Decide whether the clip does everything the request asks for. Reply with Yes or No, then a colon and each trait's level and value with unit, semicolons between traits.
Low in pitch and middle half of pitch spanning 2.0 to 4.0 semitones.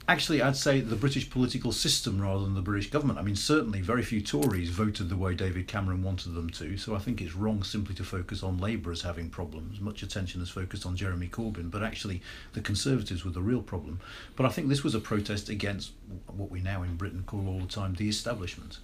Yes: low, 100 Hz; average, 3.3 semitones